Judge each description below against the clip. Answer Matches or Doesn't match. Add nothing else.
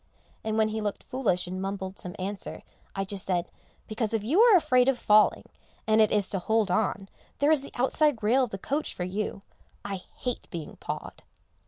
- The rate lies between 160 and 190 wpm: Doesn't match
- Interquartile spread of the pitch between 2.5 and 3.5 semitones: Doesn't match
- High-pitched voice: Matches